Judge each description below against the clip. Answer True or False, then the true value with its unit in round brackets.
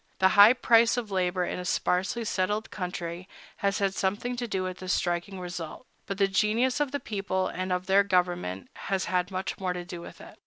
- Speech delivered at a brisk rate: True (210 wpm)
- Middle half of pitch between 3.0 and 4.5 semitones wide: False (2.4 semitones)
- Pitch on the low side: False (190 Hz)